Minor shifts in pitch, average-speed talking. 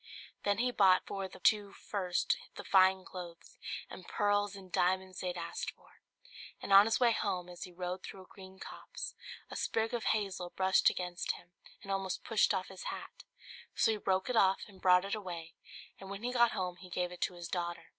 No: narrow, 2.1 semitones; fast, 210 wpm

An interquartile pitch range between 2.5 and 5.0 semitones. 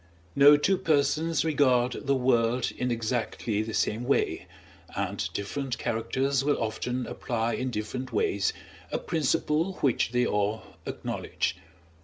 Yes: average, 3.6 semitones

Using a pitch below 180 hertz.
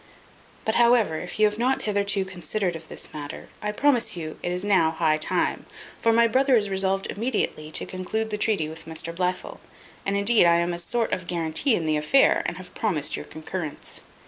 No: high, 190 Hz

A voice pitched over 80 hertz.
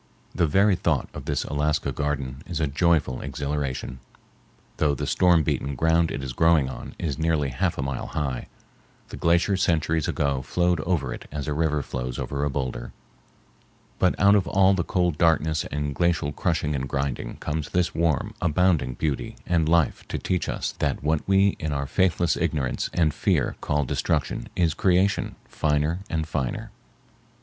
No: very low, 75 Hz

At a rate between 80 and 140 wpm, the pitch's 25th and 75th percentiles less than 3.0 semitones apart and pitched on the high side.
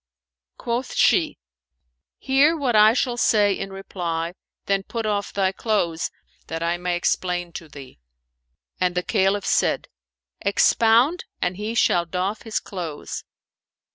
No: slow, 135 wpm; average, 4.1 semitones; high, 195 Hz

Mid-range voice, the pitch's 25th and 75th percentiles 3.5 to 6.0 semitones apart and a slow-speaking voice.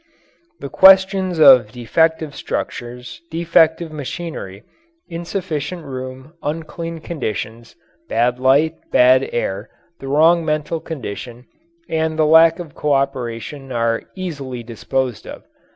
Yes: medium, 145 Hz; average, 4.7 semitones; slow, 105 wpm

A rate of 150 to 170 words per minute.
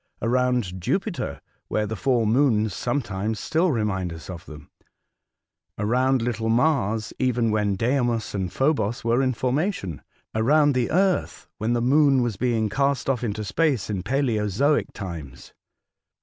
No: average, 140 wpm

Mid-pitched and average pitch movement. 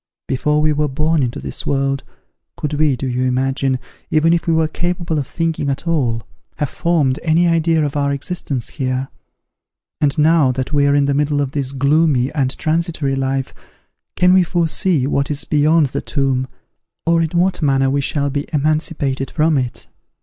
Yes: medium, 145 Hz; average, 3.0 semitones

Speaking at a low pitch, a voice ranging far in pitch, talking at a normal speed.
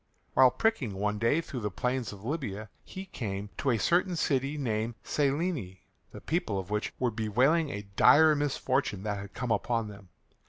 Yes: low, 120 Hz; wide, 5.7 semitones; average, 175 wpm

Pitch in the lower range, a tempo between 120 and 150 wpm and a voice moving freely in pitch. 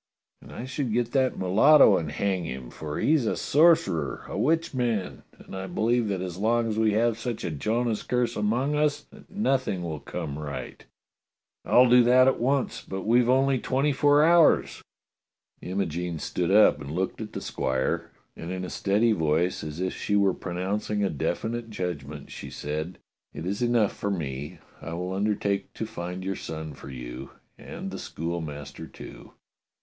No: low, 100 Hz; average, 180 wpm; wide, 6.2 semitones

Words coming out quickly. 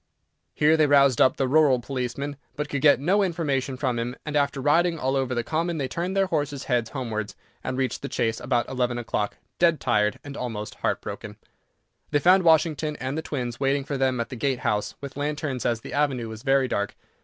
Yes: fast, 210 wpm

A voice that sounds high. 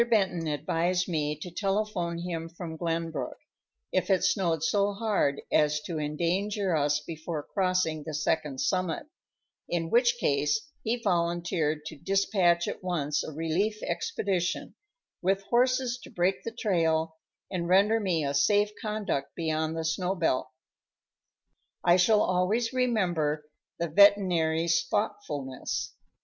No: medium, 175 Hz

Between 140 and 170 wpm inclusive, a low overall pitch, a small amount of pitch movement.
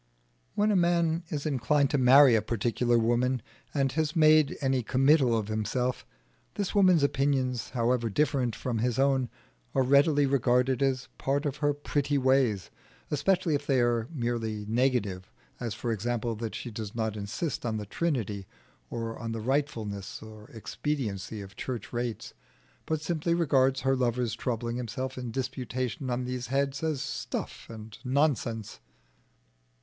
No: average, 155 wpm; low, 125 Hz; average, 3.7 semitones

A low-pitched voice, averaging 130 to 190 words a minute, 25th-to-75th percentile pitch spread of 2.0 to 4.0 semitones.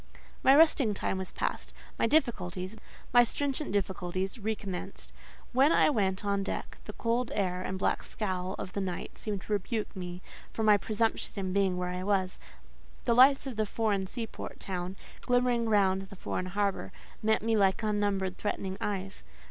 No: high, 200 Hz; average, 165 wpm; average, 3.1 semitones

